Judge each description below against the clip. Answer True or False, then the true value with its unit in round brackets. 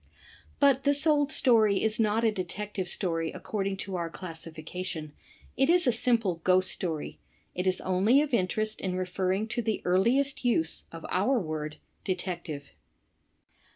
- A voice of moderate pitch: False (195 Hz)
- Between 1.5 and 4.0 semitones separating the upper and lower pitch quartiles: False (4.7 semitones)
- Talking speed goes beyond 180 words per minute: False (155 wpm)